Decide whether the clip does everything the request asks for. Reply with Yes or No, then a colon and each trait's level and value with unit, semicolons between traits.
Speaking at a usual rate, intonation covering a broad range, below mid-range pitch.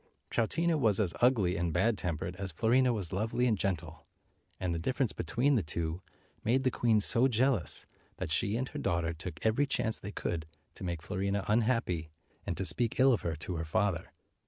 Yes: average, 195 wpm; wide, 5.8 semitones; low, 100 Hz